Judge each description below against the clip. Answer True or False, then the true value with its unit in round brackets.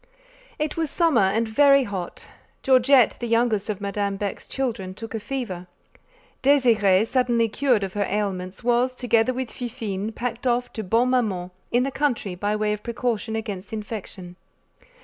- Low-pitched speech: False (225 Hz)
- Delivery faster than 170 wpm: False (160 wpm)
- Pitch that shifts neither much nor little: True (3.7 semitones)